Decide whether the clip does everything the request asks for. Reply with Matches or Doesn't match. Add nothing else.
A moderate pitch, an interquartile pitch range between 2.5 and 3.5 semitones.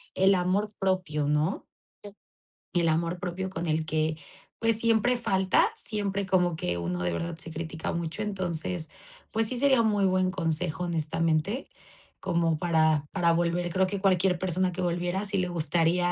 Matches